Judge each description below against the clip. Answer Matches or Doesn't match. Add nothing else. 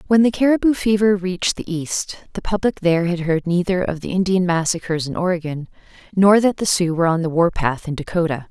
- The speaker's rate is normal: Doesn't match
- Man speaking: Doesn't match